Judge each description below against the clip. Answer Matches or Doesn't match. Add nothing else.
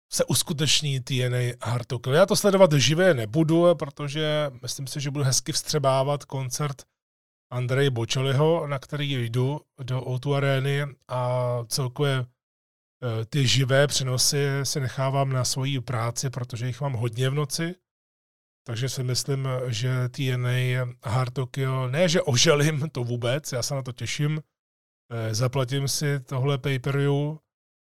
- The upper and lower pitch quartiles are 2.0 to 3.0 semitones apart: Matches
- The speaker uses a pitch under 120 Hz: Doesn't match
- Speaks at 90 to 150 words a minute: Matches